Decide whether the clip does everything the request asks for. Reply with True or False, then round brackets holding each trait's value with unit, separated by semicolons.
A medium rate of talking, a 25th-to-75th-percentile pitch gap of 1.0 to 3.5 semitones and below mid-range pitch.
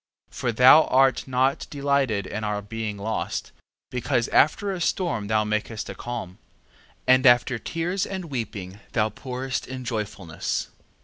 False (145 wpm; 4.0 semitones; 120 Hz)